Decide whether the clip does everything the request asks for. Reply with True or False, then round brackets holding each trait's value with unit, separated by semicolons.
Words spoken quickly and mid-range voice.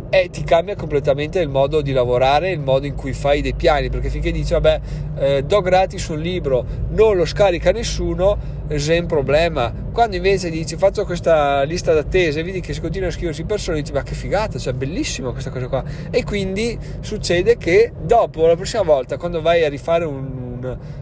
True (195 wpm; 155 Hz)